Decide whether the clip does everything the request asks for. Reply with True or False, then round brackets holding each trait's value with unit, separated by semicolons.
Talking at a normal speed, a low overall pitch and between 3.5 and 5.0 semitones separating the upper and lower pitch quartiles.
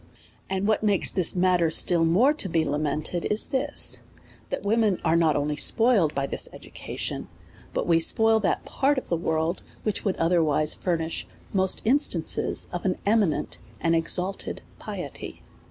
False (160 wpm; 180 Hz; 4.5 semitones)